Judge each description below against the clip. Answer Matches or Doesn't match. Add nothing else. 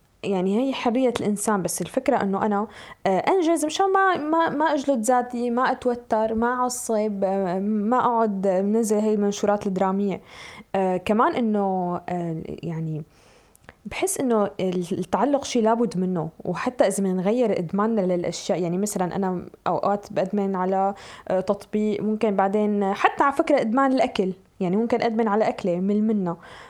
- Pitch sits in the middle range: Doesn't match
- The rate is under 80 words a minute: Doesn't match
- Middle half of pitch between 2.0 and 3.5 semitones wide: Doesn't match